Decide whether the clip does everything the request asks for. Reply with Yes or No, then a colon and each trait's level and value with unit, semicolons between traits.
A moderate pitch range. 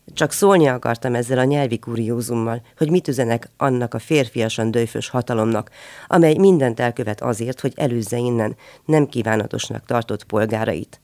Yes: average, 3.5 semitones